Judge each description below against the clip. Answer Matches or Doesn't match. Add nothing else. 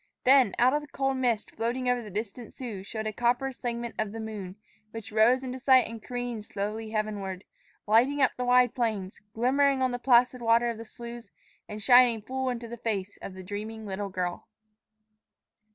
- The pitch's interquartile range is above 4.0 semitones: Doesn't match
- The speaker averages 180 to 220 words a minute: Matches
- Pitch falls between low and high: Doesn't match